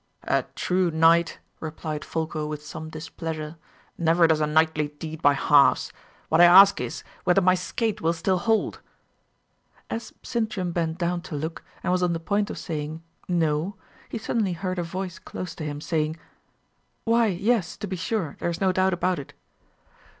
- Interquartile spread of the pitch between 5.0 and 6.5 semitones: No, average, 2.8 semitones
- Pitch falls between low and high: Yes, medium, 170 Hz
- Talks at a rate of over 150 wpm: Yes, average, 175 wpm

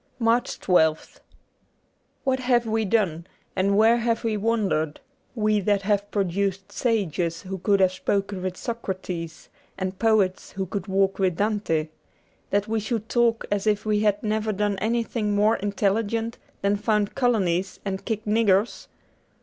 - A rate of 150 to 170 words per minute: Yes, average, 155 wpm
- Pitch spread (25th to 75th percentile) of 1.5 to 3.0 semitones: Yes, average, 2.7 semitones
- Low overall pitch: No, high, 205 Hz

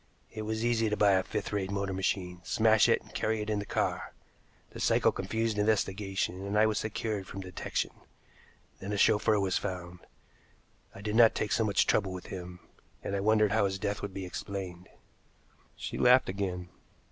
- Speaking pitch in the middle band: No, low, 100 Hz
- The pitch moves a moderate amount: No, narrow, 2.3 semitones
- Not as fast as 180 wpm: No, average, 190 wpm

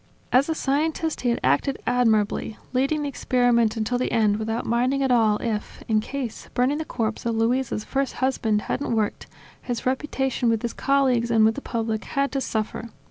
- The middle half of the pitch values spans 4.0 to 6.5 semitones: No, average, 3.2 semitones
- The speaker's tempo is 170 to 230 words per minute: Yes, average, 190 wpm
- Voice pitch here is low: No, high, 245 Hz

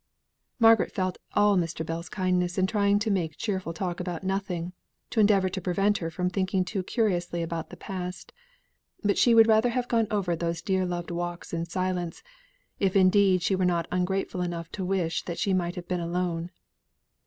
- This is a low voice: No, medium, 185 Hz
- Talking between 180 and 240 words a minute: Yes, average, 190 wpm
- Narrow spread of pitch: Yes, narrow, 2.3 semitones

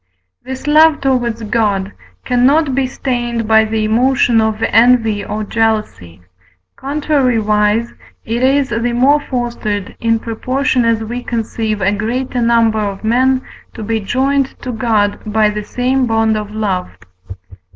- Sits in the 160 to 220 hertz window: No, high, 230 Hz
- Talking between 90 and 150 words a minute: Yes, average, 140 wpm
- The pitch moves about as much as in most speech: Yes, average, 3.0 semitones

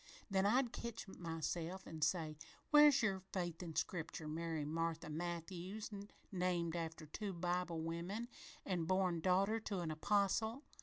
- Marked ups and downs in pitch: No, average, 3.1 semitones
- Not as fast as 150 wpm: Yes, average, 140 wpm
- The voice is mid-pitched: Yes, medium, 175 Hz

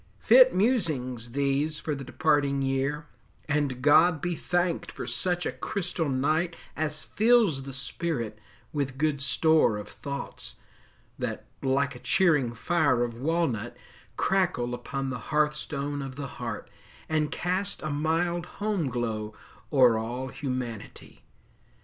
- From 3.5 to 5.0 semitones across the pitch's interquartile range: Yes, average, 4.2 semitones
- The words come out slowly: Yes, slow, 130 wpm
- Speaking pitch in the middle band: Yes, medium, 145 Hz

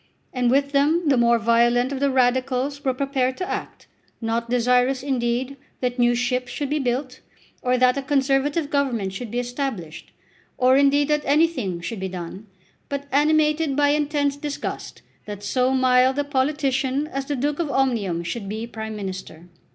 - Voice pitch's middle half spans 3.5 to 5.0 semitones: No, average, 3.0 semitones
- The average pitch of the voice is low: No, very high, 260 Hz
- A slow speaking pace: No, average, 170 wpm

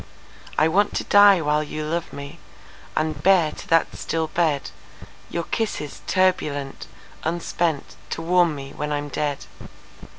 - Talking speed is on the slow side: Yes, slow, 125 wpm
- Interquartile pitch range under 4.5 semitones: Yes, average, 2.8 semitones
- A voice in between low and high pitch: Yes, medium, 160 Hz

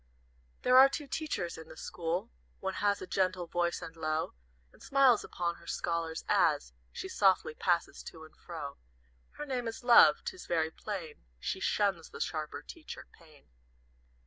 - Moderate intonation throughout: No, wide, 5.7 semitones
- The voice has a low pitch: No, medium, 175 Hz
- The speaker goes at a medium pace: Yes, average, 165 wpm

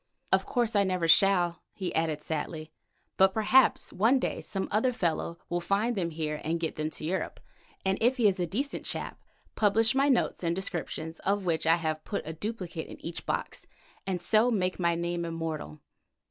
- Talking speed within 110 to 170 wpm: No, average, 190 wpm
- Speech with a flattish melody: No, average, 4.2 semitones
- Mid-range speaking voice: Yes, medium, 180 Hz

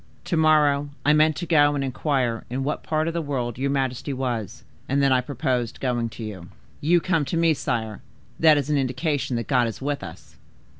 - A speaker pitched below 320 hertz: Yes, medium, 140 Hz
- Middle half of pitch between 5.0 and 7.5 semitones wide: No, average, 3.4 semitones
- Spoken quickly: Yes, fast, 210 wpm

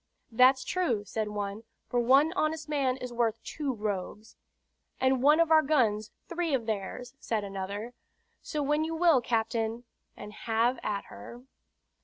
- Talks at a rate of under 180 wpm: Yes, average, 155 wpm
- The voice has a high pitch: Yes, high, 245 Hz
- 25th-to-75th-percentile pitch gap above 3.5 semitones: Yes, wide, 5.4 semitones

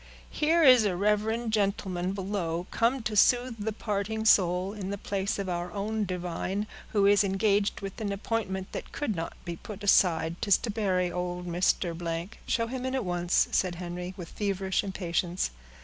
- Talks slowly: No, average, 175 wpm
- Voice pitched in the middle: No, high, 195 Hz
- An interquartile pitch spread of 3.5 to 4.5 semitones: No, average, 3.1 semitones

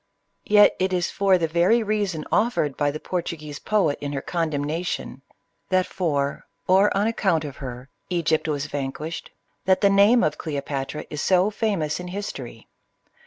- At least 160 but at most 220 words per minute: Yes, average, 175 wpm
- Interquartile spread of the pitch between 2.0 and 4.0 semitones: No, average, 4.9 semitones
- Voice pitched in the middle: Yes, medium, 170 Hz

